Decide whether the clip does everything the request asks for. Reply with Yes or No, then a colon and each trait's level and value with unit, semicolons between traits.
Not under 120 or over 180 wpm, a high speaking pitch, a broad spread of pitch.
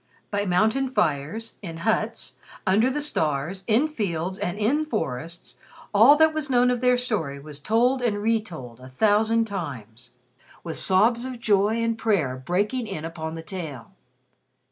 Yes: average, 155 wpm; high, 205 Hz; wide, 6.4 semitones